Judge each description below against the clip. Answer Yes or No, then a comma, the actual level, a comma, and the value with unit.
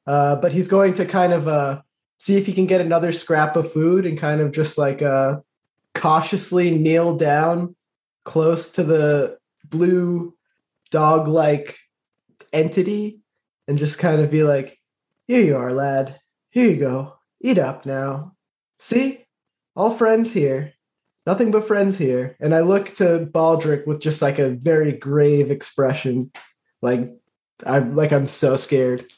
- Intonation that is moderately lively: Yes, average, 4.2 semitones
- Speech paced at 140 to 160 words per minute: Yes, average, 155 wpm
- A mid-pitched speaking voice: Yes, medium, 155 Hz